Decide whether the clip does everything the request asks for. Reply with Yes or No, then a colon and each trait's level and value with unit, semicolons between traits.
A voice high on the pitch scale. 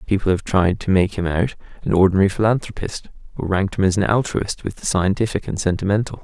No: very low, 95 Hz